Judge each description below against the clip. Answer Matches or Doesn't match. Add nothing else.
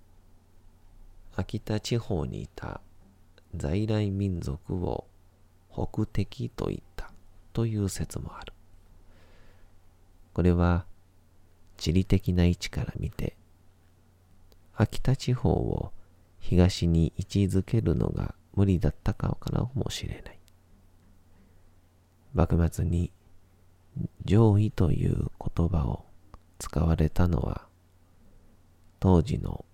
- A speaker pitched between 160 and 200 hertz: Doesn't match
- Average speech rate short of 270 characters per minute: Matches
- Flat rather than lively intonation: Matches